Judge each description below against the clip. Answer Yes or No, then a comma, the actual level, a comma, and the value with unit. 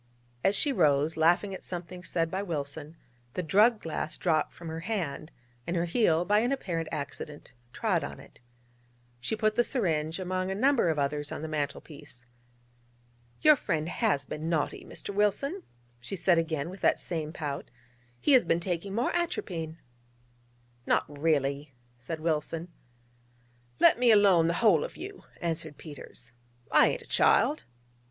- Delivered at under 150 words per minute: No, average, 160 wpm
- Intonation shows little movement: No, average, 4.7 semitones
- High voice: No, medium, 170 Hz